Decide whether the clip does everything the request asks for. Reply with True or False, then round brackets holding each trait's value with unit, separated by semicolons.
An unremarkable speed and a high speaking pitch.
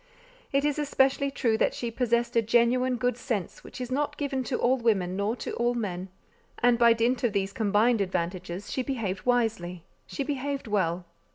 True (180 wpm; 235 Hz)